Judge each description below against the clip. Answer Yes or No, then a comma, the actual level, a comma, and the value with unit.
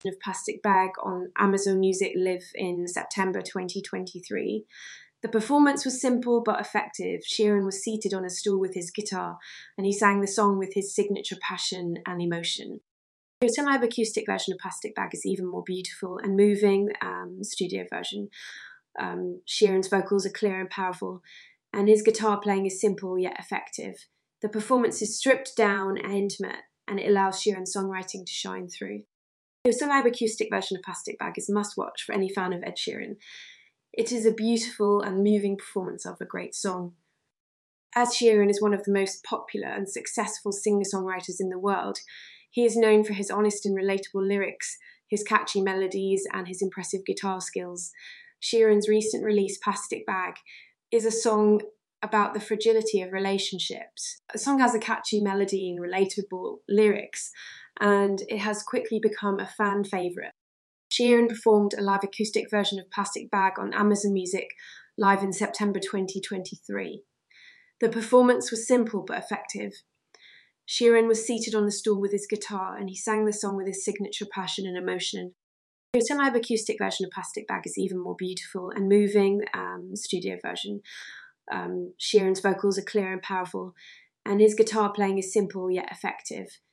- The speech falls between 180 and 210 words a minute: No, average, 170 wpm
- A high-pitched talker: Yes, high, 200 Hz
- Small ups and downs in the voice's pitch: Yes, narrow, 2.2 semitones